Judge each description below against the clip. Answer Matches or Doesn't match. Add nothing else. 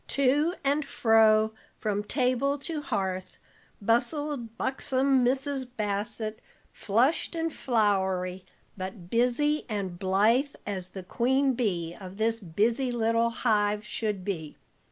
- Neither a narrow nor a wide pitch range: Matches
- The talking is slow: Matches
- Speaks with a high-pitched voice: Matches